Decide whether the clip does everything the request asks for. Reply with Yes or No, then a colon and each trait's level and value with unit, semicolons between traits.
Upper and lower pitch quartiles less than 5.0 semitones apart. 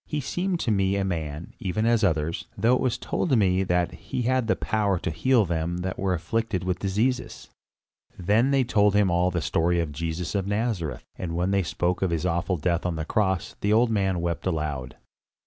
Yes: average, 4.1 semitones